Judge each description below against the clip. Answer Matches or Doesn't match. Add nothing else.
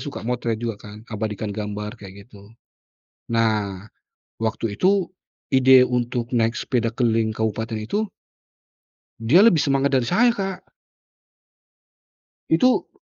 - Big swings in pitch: Doesn't match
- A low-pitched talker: Matches